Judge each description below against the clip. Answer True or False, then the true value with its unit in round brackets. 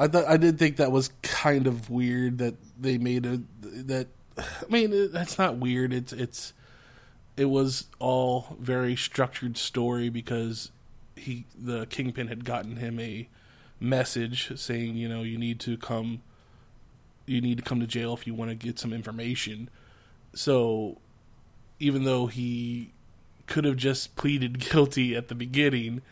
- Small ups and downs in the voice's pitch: True (1.9 semitones)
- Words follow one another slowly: False (160 wpm)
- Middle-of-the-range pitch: False (125 Hz)